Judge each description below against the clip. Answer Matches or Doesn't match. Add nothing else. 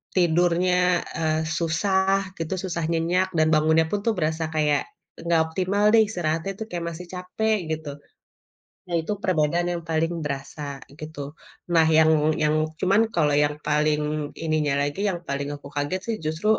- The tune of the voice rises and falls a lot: Doesn't match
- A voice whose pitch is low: Doesn't match